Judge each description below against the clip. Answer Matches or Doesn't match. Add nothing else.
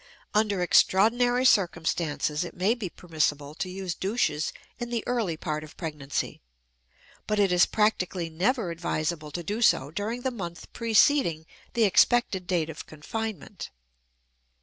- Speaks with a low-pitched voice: Doesn't match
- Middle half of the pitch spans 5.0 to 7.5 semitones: Matches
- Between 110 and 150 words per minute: Matches